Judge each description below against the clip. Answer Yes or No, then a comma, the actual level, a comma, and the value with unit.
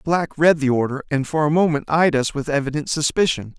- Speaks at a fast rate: Yes, fast, 235 wpm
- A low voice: No, medium, 150 Hz